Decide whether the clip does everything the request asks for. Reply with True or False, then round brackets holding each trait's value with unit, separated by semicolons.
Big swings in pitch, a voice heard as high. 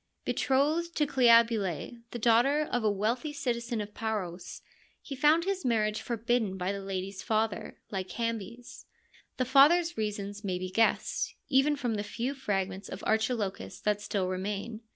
False (4.2 semitones; 225 Hz)